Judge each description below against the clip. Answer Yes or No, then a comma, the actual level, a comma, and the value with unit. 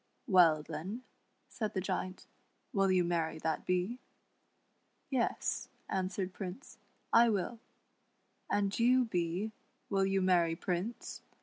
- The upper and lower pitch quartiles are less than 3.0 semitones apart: No, average, 3.4 semitones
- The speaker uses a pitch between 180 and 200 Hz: Yes, high, 190 Hz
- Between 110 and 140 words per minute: Yes, slow, 135 wpm